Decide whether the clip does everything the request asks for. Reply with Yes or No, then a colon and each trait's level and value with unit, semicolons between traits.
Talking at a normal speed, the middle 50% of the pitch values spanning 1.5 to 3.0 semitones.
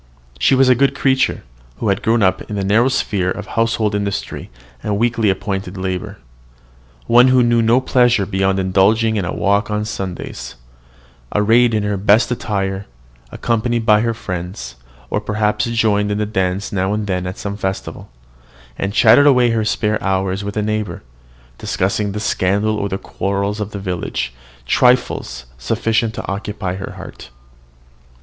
Yes: average, 165 wpm; average, 2.7 semitones